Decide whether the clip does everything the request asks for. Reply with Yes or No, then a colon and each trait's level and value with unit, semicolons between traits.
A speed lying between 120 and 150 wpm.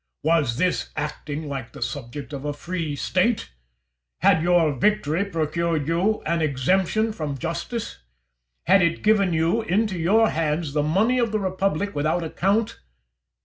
Yes: average, 145 wpm